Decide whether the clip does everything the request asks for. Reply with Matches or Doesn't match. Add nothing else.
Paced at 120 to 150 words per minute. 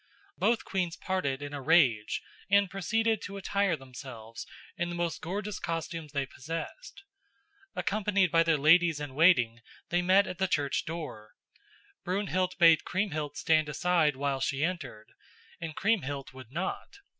Matches